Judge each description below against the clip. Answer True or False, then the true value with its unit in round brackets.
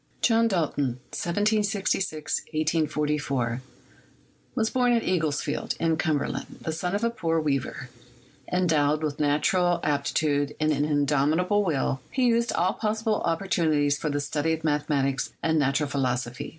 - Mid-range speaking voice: True (155 Hz)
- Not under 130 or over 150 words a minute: True (145 wpm)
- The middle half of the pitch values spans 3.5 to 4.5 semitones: True (4.2 semitones)